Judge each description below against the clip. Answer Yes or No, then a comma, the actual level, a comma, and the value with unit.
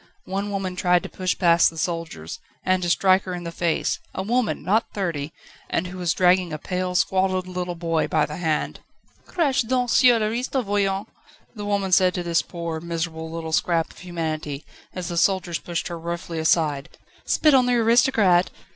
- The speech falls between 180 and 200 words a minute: Yes, average, 185 wpm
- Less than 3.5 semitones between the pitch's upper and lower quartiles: Yes, average, 2.9 semitones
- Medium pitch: Yes, medium, 180 Hz